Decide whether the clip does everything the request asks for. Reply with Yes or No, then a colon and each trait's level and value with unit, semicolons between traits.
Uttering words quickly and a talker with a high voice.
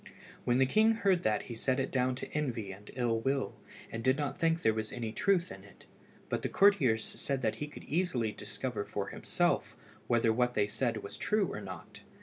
No: fast, 210 wpm; low, 125 Hz